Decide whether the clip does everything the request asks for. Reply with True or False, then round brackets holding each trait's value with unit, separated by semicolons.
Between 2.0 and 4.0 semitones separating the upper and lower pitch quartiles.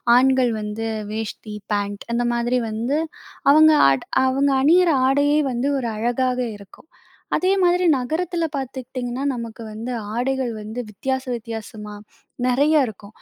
True (3.7 semitones)